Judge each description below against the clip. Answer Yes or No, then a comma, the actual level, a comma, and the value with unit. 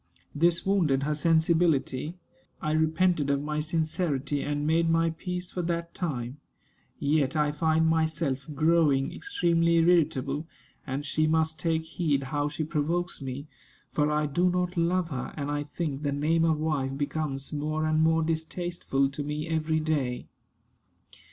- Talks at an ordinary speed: Yes, average, 150 wpm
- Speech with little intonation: Yes, narrow, 2.3 semitones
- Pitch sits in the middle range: Yes, medium, 155 Hz